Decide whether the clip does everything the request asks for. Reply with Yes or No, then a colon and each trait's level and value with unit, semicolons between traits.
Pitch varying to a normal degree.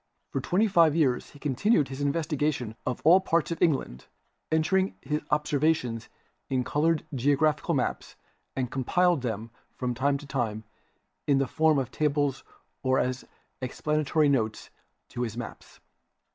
Yes: average, 3.6 semitones